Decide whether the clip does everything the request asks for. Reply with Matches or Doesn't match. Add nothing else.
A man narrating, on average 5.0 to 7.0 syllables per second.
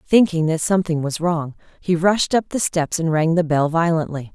Doesn't match